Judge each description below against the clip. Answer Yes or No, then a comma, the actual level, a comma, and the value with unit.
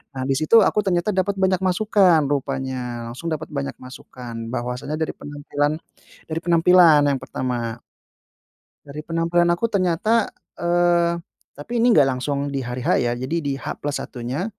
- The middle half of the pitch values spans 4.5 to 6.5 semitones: Yes, average, 5.0 semitones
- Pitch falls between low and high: Yes, medium, 150 Hz